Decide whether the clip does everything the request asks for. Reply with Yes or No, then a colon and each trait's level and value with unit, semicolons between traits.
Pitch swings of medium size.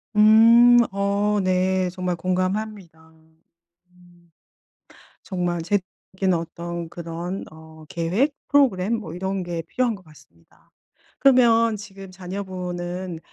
Yes: average, 3.1 semitones